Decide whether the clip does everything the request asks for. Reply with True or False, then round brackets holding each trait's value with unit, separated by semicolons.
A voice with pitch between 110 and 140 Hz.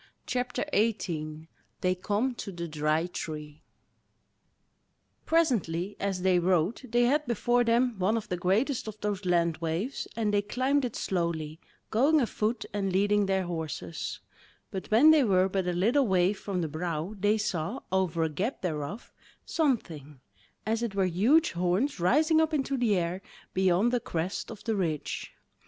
False (195 Hz)